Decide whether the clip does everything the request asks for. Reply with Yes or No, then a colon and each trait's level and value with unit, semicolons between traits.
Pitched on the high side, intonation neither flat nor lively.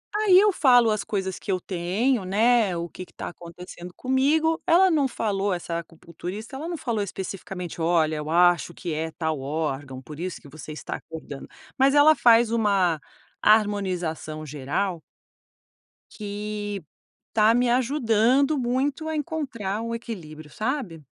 No: high, 205 Hz; wide, 6.5 semitones